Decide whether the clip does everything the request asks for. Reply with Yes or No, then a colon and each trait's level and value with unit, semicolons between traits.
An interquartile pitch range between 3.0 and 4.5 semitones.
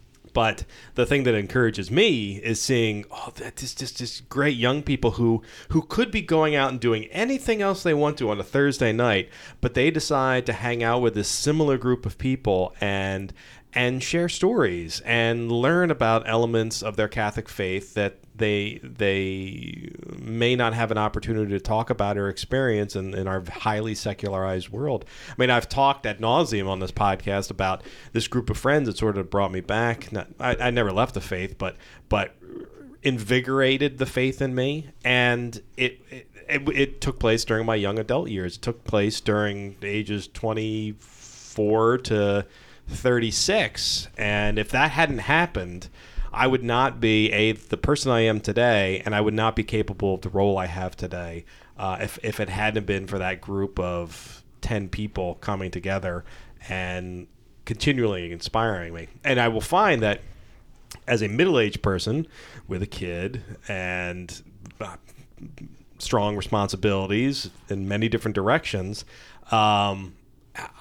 Yes: average, 4.2 semitones